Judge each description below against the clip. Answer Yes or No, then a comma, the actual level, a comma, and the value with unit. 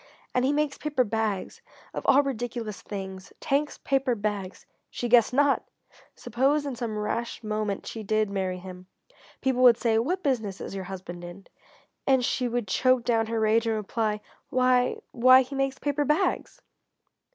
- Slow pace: No, average, 165 wpm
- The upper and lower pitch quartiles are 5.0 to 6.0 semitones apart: No, average, 3.8 semitones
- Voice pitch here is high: Yes, high, 235 Hz